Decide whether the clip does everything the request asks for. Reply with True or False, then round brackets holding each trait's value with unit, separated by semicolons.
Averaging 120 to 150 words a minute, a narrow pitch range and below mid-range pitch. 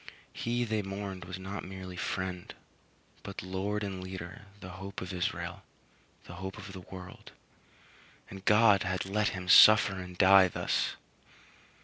True (145 wpm; 1.5 semitones; 95 Hz)